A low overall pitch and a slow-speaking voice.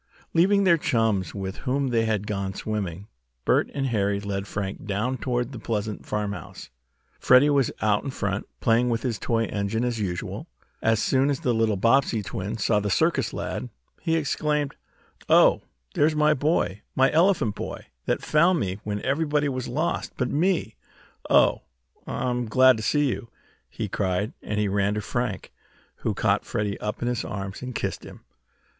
No: low, 115 Hz; average, 175 wpm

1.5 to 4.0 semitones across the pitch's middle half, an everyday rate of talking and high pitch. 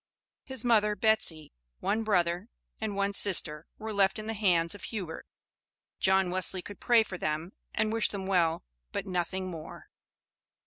Yes: average, 3.4 semitones; average, 155 wpm; high, 195 Hz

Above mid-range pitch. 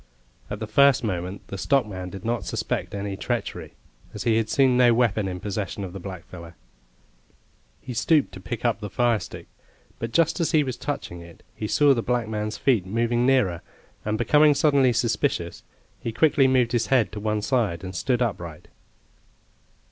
No: low, 115 Hz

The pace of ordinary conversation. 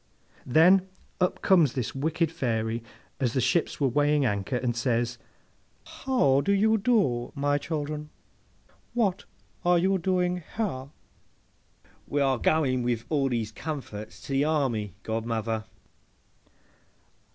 No: slow, 120 wpm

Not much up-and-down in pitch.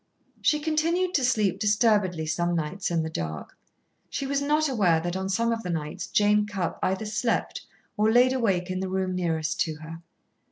No: average, 5.2 semitones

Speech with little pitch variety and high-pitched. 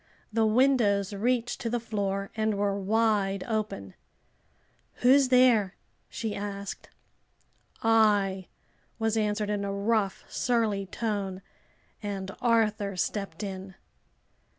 Yes: narrow, 2.3 semitones; high, 210 Hz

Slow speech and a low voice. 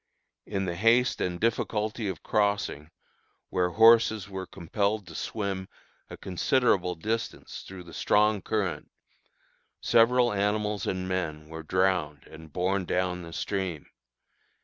Yes: slow, 125 wpm; very low, 95 Hz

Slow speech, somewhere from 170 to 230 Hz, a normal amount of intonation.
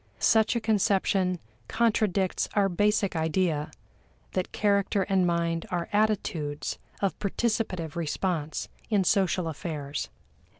Yes: slow, 110 wpm; medium, 185 Hz; average, 3.7 semitones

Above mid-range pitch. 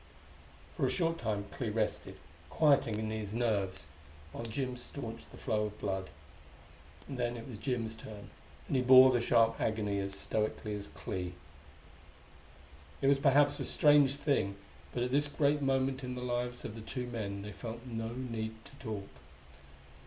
No: low, 115 Hz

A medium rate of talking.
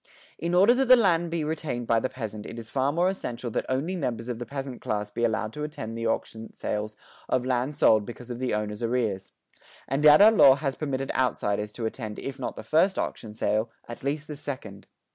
No: fast, 220 wpm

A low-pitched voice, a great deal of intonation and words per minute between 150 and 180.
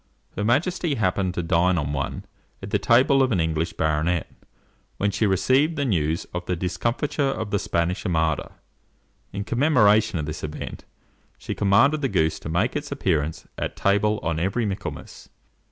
Yes: low, 100 Hz; wide, 6.3 semitones; average, 170 wpm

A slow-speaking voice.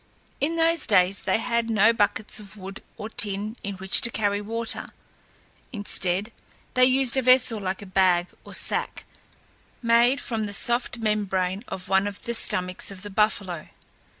No: average, 165 wpm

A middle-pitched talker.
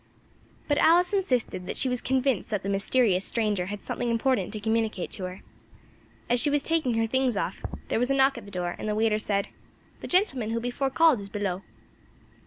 No: high, 230 Hz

